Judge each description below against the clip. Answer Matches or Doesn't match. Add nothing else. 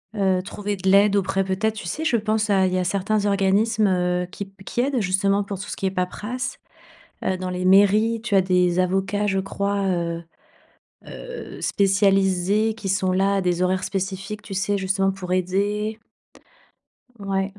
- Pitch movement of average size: Doesn't match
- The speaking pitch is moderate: Doesn't match